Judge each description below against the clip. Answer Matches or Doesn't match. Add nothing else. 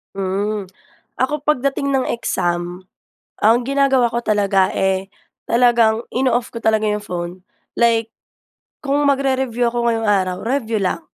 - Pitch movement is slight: Doesn't match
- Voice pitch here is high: Matches